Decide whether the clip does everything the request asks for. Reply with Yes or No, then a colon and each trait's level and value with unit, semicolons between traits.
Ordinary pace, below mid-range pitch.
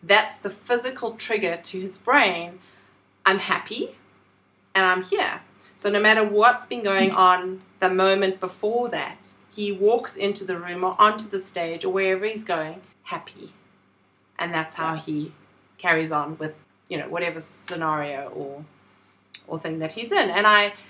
No: average, 160 wpm; medium, 185 Hz